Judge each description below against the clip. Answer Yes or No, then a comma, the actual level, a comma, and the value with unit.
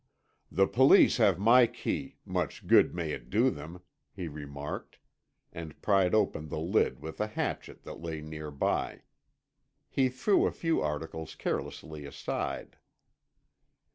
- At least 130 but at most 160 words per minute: Yes, slow, 135 wpm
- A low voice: Yes, very low, 80 Hz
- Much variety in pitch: Yes, wide, 5.9 semitones